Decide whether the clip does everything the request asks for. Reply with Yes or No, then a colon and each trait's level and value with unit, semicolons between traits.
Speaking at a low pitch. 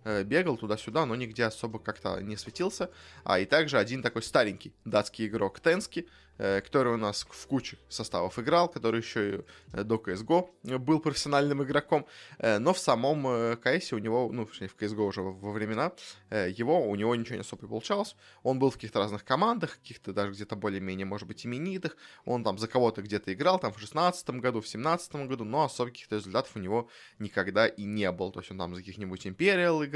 Yes: low, 115 Hz